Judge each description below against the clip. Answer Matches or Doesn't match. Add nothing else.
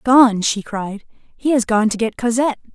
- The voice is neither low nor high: Doesn't match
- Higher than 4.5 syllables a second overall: Doesn't match